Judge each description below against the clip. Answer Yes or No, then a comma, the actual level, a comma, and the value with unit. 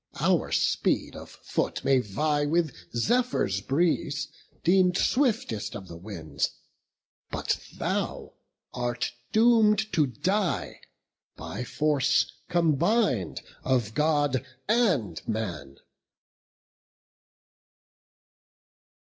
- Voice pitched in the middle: Yes, medium, 145 Hz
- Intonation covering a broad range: Yes, wide, 8.7 semitones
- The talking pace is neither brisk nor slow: No, slow, 85 wpm